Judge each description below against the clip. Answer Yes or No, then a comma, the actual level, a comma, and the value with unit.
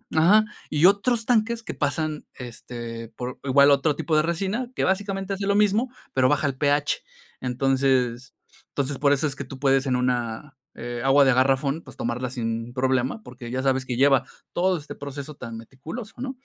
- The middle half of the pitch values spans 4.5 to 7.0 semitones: Yes, average, 4.9 semitones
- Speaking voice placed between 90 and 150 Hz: Yes, medium, 140 Hz